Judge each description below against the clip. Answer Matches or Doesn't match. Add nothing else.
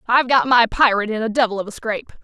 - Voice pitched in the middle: Doesn't match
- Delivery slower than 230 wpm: Doesn't match